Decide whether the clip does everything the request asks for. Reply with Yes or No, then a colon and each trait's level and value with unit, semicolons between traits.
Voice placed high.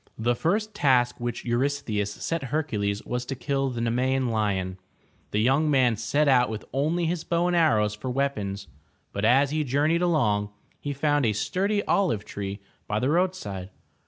No: low, 130 Hz